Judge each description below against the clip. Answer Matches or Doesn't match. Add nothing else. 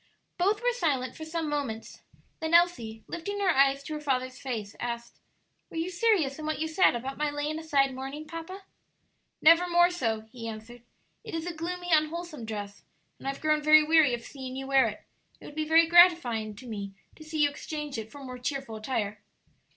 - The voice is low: Doesn't match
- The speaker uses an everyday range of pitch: Matches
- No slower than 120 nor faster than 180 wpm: Doesn't match